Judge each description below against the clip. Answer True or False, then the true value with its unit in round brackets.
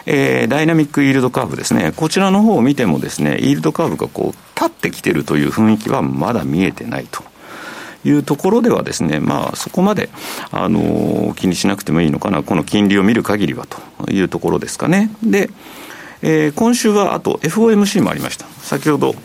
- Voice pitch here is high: False (165 Hz)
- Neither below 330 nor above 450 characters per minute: True (420 characters per minute)